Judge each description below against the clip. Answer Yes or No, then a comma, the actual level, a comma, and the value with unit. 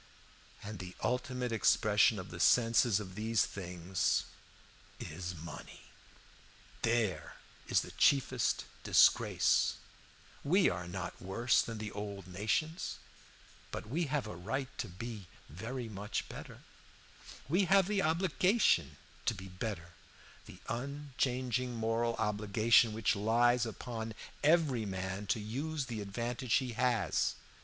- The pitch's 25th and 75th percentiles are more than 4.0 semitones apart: Yes, average, 4.4 semitones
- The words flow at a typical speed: No, slow, 125 wpm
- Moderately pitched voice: No, low, 115 Hz